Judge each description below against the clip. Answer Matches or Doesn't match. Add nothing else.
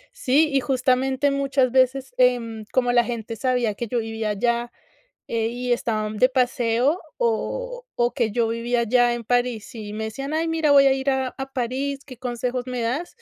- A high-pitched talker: Matches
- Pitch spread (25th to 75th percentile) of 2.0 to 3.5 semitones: Matches